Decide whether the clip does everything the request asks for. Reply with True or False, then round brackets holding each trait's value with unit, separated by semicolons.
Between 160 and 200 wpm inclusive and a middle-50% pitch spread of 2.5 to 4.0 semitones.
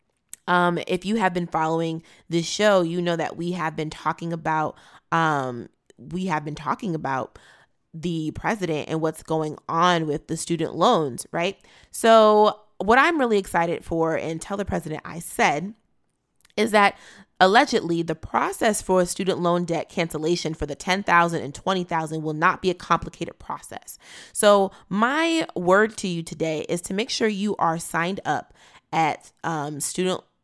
True (170 wpm; 3.3 semitones)